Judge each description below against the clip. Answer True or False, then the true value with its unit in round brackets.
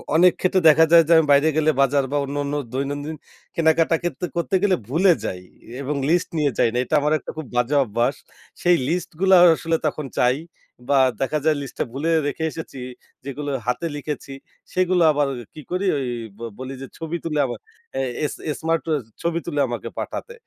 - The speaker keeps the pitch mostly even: False (3.1 semitones)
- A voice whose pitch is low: False (150 Hz)